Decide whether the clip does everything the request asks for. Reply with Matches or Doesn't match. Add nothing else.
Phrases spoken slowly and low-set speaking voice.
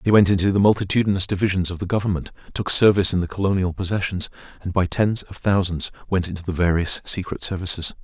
Doesn't match